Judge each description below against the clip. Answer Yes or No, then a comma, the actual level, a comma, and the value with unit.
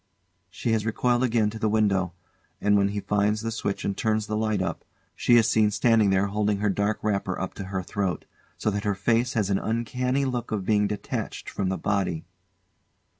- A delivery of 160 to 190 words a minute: No, fast, 205 wpm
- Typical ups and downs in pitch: No, narrow, 2.0 semitones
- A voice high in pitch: No, low, 105 Hz